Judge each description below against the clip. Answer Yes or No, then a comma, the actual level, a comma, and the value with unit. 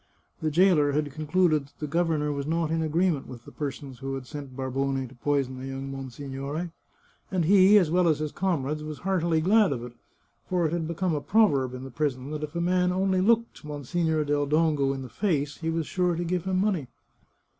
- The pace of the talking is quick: Yes, fast, 220 wpm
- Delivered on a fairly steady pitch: No, average, 4.2 semitones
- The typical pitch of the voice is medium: Yes, medium, 155 Hz